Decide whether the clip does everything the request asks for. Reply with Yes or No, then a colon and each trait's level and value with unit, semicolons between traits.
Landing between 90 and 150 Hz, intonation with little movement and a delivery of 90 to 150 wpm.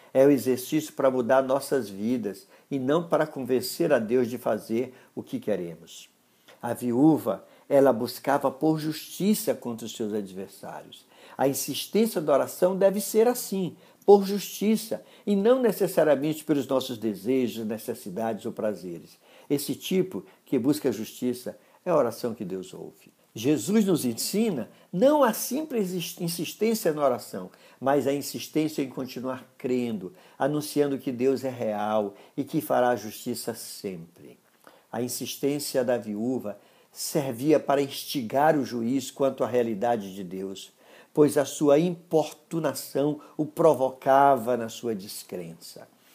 No: low, 135 Hz; average, 4.7 semitones; average, 140 wpm